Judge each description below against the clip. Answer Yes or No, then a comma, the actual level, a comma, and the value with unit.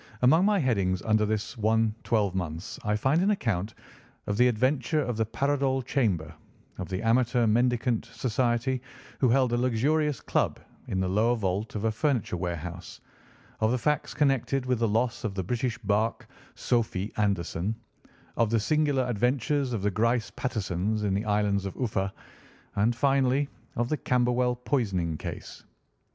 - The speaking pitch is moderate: No, low, 115 Hz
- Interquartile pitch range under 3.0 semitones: No, average, 3.8 semitones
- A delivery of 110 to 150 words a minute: No, average, 160 wpm